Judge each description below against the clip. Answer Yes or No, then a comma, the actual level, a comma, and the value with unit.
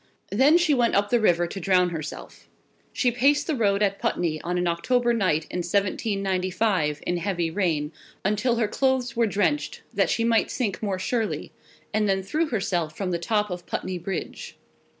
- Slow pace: No, average, 180 wpm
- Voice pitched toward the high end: Yes, high, 200 Hz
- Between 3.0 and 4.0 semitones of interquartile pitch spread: No, average, 4.8 semitones